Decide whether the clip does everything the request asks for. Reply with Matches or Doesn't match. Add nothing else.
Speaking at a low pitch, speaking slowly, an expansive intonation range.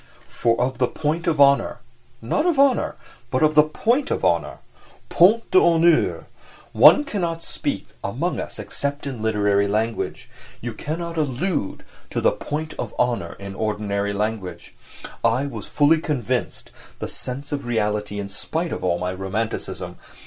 Doesn't match